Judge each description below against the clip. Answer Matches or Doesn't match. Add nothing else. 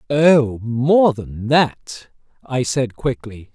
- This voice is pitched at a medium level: Doesn't match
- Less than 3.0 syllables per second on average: Matches